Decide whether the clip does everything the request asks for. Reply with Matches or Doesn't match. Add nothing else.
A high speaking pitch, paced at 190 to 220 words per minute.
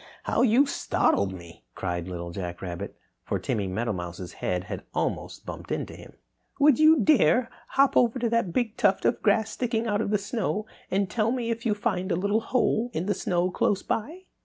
Matches